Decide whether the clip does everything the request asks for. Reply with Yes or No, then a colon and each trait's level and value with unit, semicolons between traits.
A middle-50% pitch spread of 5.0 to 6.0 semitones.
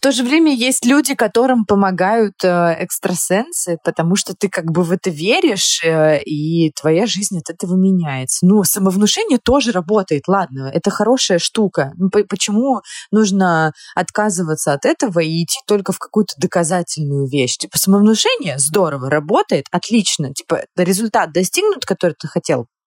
No: average, 4.4 semitones